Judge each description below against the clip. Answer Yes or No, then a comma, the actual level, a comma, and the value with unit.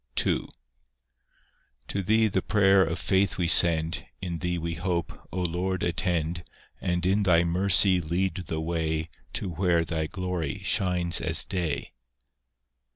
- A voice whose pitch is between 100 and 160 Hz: No, very low, 90 Hz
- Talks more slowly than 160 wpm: Yes, average, 140 wpm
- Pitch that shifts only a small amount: Yes, narrow, 2.1 semitones